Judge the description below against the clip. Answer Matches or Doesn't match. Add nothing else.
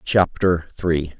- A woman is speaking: Doesn't match